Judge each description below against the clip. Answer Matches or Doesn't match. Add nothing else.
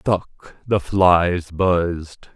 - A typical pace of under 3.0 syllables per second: Matches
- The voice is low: Matches